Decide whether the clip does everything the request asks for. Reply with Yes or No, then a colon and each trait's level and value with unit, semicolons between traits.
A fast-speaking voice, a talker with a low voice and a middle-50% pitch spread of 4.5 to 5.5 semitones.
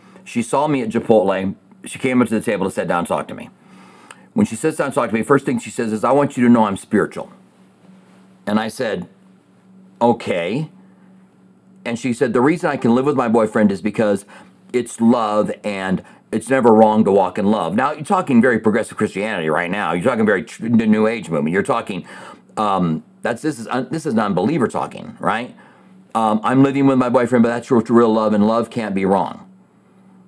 Yes: fast, 210 wpm; low, 120 Hz; average, 4.9 semitones